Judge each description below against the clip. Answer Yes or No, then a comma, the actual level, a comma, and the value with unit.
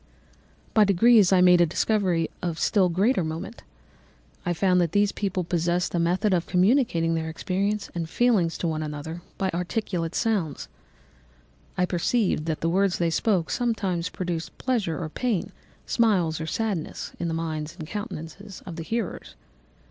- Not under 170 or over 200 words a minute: No, average, 160 wpm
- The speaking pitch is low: No, medium, 180 Hz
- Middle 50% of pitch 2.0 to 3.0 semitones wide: No, average, 3.6 semitones